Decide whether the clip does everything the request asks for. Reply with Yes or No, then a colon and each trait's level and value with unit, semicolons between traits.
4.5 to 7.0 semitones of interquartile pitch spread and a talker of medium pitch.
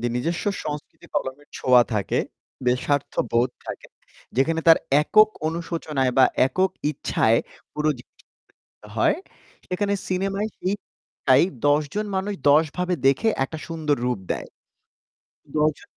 Yes: wide, 5.6 semitones; medium, 155 Hz